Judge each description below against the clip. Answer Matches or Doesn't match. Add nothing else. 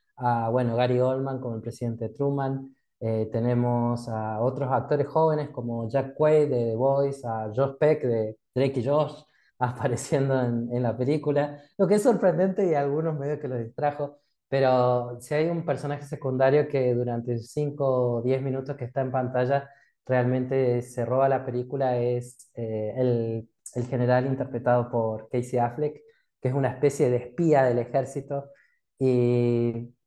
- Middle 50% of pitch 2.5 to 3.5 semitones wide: Matches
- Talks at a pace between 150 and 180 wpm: Matches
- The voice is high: Doesn't match